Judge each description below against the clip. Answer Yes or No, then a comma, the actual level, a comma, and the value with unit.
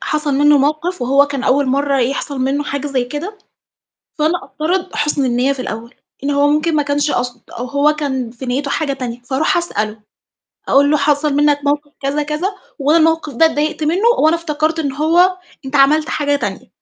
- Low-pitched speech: No, very high, 290 Hz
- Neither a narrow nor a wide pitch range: No, narrow, 2.1 semitones